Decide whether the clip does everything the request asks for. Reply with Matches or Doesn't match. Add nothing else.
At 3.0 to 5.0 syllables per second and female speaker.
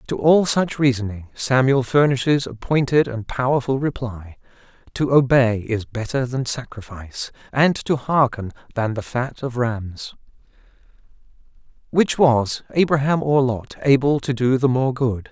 Doesn't match